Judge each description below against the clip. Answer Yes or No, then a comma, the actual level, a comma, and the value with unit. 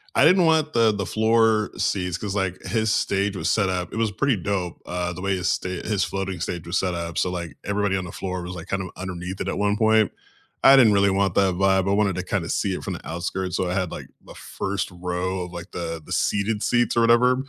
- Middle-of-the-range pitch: No, very low, 95 Hz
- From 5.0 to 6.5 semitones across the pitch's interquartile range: No, average, 2.8 semitones